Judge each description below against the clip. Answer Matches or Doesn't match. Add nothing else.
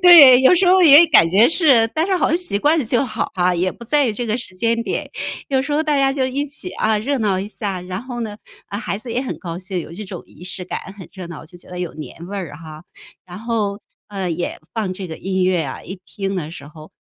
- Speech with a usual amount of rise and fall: Doesn't match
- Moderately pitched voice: Doesn't match